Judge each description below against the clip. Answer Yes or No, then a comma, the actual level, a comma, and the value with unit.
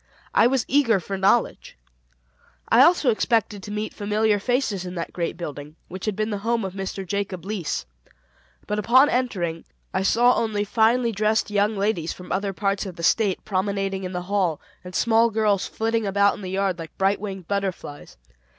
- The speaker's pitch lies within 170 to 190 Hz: No, high, 200 Hz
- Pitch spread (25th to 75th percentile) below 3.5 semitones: Yes, average, 2.9 semitones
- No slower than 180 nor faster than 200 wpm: Yes, average, 185 wpm